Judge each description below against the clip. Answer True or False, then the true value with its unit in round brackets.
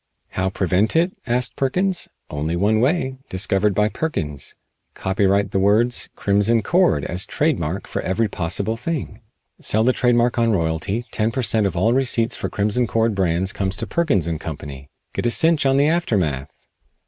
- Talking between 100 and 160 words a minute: False (175 wpm)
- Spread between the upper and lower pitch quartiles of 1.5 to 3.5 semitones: False (4.9 semitones)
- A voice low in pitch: True (110 Hz)